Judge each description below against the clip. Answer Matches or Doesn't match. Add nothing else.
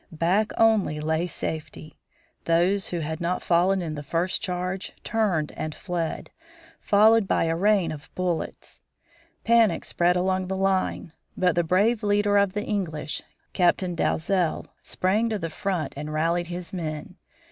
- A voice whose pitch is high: Doesn't match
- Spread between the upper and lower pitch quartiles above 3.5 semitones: Doesn't match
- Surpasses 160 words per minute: Doesn't match